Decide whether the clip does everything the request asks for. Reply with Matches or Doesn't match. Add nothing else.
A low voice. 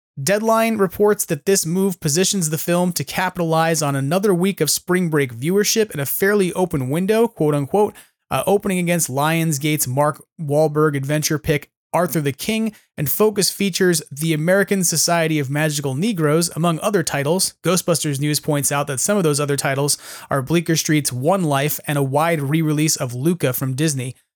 Doesn't match